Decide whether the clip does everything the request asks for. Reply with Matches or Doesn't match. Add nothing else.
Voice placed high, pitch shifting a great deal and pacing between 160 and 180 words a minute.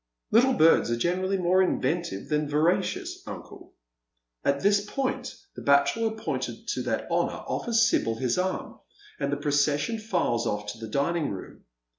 Doesn't match